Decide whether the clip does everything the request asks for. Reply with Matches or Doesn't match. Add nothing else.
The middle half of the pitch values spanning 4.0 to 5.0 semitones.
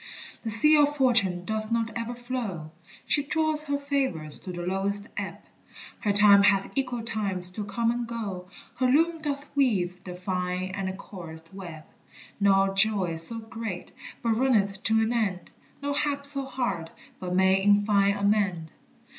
Matches